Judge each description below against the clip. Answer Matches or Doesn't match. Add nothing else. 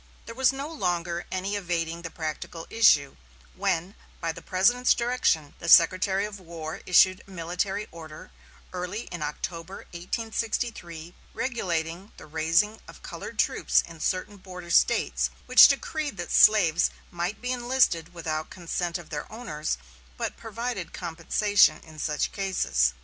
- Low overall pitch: Doesn't match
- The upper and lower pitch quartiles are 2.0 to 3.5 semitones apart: Doesn't match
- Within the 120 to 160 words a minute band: Matches